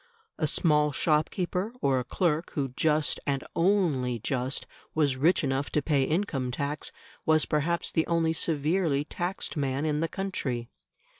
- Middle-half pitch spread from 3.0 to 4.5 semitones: Yes, average, 3.4 semitones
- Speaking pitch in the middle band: Yes, medium, 150 Hz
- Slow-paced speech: No, average, 150 wpm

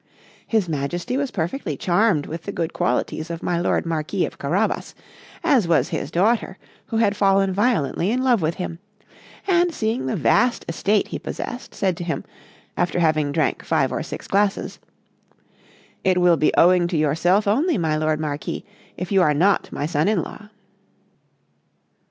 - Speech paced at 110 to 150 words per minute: No, average, 170 wpm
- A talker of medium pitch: Yes, medium, 180 Hz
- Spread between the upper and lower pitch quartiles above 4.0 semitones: Yes, average, 4.7 semitones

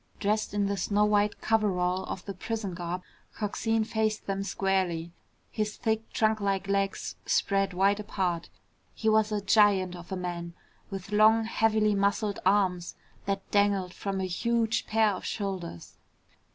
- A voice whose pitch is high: Yes, high, 200 Hz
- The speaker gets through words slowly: No, average, 150 wpm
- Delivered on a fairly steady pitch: Yes, narrow, 2.3 semitones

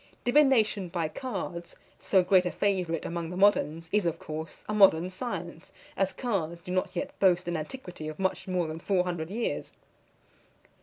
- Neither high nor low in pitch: Yes, medium, 180 Hz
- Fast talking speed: No, average, 170 wpm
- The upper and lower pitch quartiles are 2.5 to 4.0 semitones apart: Yes, average, 3.0 semitones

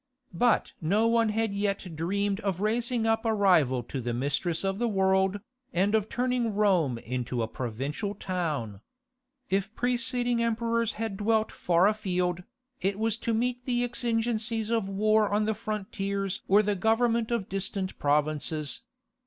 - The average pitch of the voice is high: Yes, high, 205 Hz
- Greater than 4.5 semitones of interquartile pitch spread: No, average, 4.1 semitones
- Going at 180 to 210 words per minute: No, average, 155 wpm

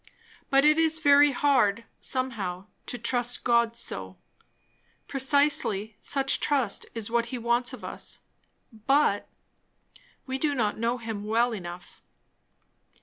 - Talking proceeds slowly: Yes, slow, 125 wpm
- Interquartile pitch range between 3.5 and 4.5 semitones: Yes, average, 4.0 semitones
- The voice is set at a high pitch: Yes, high, 240 Hz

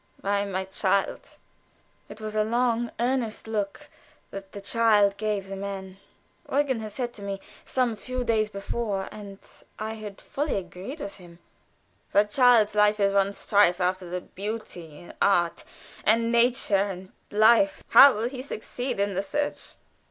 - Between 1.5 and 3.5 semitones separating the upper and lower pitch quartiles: Yes, average, 2.9 semitones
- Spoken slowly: No, average, 160 wpm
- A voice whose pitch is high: Yes, high, 210 Hz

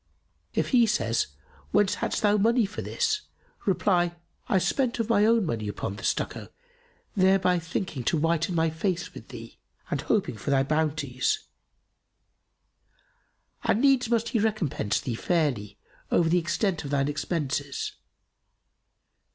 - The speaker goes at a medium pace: Yes, average, 145 wpm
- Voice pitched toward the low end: No, medium, 175 Hz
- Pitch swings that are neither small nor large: No, wide, 6.5 semitones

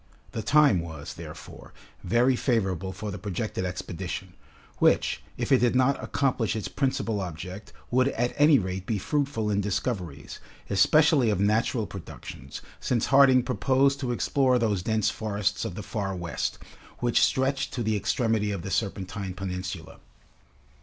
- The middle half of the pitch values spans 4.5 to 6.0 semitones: Yes, average, 5.1 semitones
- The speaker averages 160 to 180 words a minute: No, average, 150 wpm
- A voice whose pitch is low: Yes, low, 105 Hz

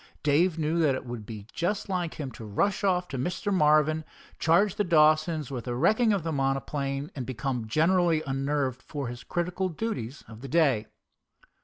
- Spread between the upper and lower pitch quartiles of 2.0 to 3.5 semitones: No, average, 4.8 semitones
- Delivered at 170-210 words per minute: Yes, average, 180 wpm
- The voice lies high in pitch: No, medium, 150 Hz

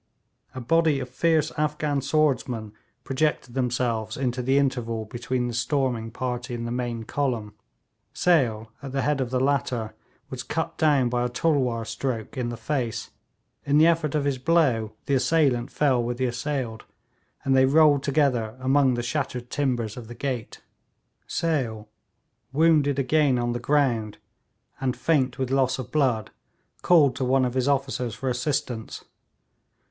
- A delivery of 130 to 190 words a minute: Yes, average, 160 wpm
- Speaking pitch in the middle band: No, low, 130 Hz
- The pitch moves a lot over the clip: No, average, 2.9 semitones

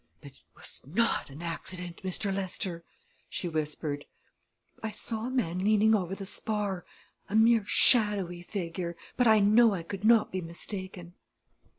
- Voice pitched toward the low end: No, high, 195 Hz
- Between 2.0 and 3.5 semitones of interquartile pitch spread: No, average, 3.9 semitones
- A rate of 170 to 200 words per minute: No, average, 155 wpm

